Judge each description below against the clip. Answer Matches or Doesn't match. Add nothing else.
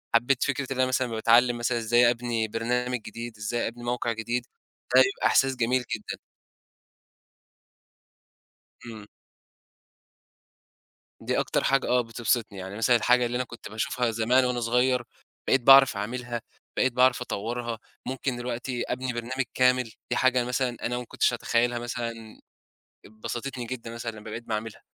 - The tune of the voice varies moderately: Doesn't match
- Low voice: Matches